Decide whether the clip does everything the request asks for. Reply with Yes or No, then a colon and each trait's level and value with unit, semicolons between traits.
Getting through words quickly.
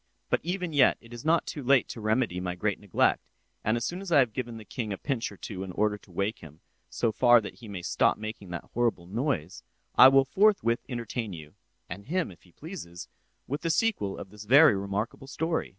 Yes: fast, 225 wpm